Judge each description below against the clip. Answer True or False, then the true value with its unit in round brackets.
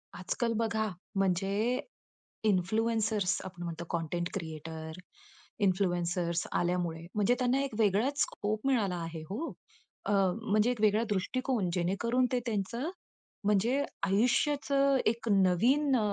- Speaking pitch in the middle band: False (205 Hz)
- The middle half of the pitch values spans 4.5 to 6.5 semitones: True (4.9 semitones)